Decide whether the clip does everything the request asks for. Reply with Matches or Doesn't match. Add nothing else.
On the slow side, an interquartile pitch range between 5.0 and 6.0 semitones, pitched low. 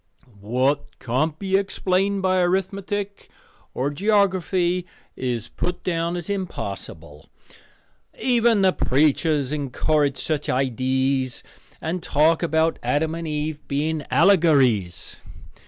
Doesn't match